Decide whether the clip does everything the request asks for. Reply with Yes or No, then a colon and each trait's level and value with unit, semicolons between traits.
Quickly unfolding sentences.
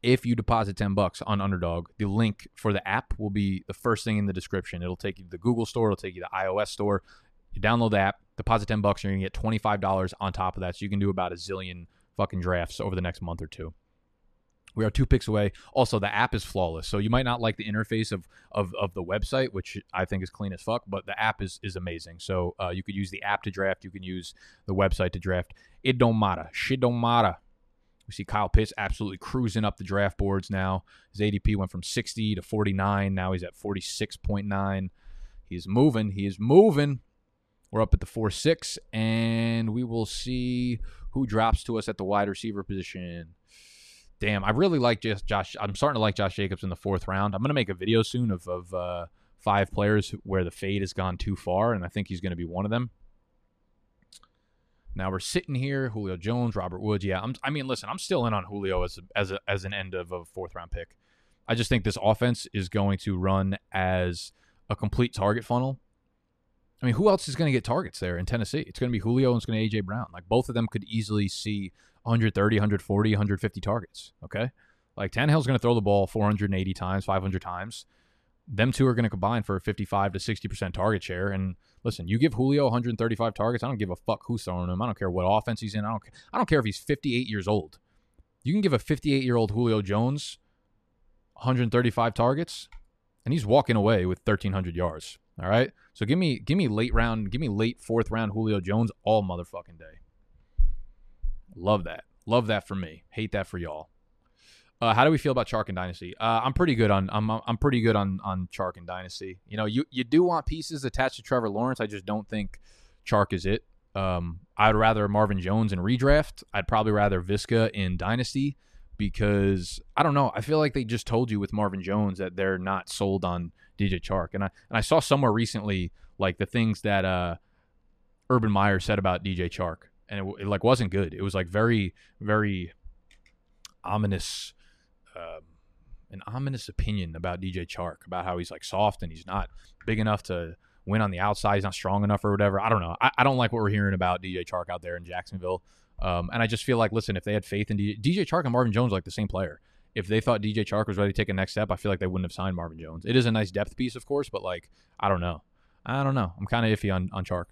Yes: fast, 235 wpm